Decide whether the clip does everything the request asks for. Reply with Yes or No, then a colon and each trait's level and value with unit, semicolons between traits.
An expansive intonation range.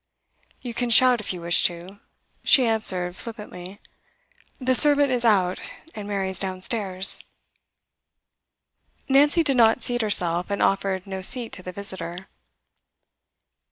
No: average, 4.6 semitones